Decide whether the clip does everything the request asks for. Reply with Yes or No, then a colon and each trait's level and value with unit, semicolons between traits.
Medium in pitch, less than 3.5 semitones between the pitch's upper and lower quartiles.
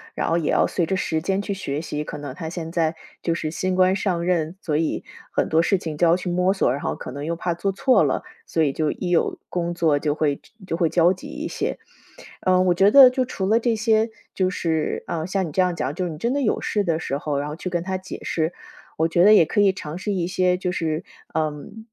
Yes: medium, 175 Hz; average, 3.1 semitones